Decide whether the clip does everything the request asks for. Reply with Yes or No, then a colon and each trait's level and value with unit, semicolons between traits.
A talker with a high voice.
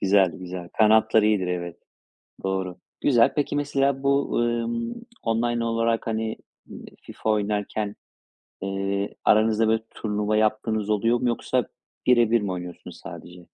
No: low, 110 Hz